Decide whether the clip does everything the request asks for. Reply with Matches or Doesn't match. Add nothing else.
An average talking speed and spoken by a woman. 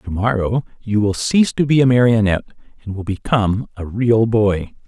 Doesn't match